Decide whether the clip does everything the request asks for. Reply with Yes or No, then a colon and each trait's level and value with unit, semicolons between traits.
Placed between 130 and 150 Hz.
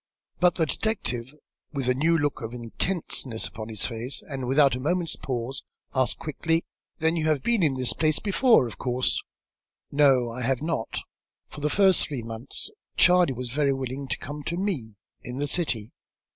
Yes: medium, 140 Hz